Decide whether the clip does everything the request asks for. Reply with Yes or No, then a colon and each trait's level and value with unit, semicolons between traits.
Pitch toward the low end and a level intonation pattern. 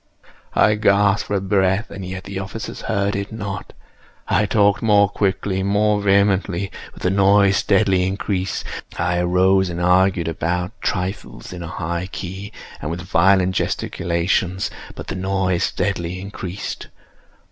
Yes: very low, 95 Hz; narrow, 1.7 semitones